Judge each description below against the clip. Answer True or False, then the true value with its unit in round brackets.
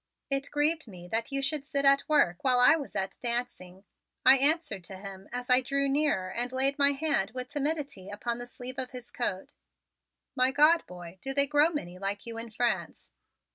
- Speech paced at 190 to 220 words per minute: True (200 wpm)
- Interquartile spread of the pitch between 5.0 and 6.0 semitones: True (5.4 semitones)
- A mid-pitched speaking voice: False (255 Hz)